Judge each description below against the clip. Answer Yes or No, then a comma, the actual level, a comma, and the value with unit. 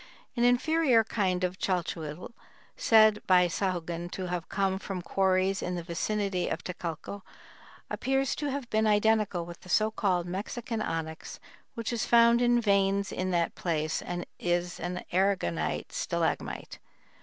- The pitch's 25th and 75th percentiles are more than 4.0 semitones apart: No, average, 3.7 semitones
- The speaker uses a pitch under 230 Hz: Yes, high, 190 Hz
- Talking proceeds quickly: No, average, 145 wpm